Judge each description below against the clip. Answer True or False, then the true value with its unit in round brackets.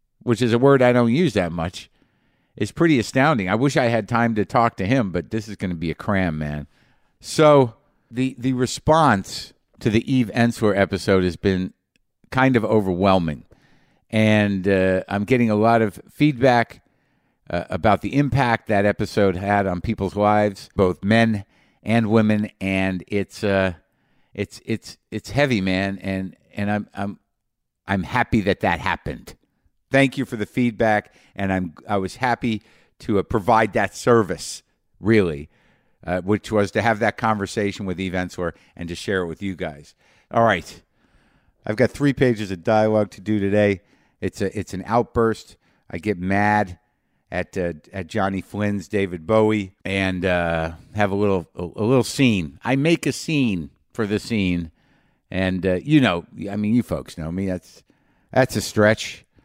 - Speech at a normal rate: True (175 wpm)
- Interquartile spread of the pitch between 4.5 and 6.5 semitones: False (3.7 semitones)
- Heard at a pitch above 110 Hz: False (105 Hz)